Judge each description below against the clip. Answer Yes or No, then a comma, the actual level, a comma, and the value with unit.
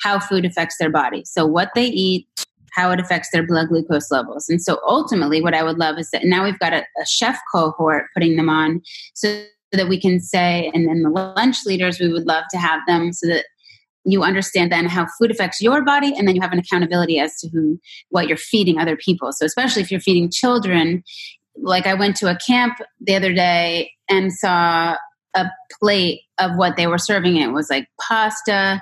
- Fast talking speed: Yes, fast, 215 wpm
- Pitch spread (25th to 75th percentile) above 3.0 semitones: No, average, 2.7 semitones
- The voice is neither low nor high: Yes, medium, 180 Hz